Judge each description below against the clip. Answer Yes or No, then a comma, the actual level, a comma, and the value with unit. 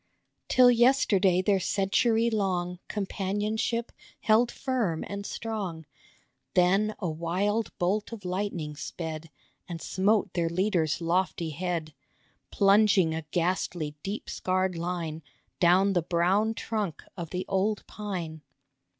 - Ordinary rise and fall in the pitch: Yes, average, 3.6 semitones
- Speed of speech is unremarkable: No, slow, 115 wpm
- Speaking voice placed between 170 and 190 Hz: Yes, medium, 185 Hz